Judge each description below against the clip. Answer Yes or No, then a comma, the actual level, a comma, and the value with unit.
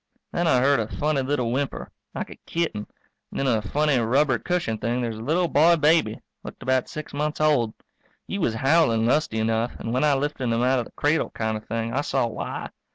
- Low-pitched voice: Yes, low, 130 Hz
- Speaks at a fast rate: Yes, fast, 220 wpm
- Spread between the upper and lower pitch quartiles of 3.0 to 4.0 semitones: No, average, 4.6 semitones